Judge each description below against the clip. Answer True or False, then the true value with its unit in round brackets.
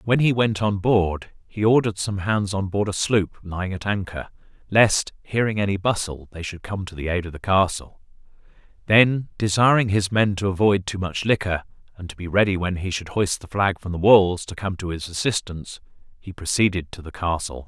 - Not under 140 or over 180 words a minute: False (205 wpm)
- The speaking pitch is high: False (95 Hz)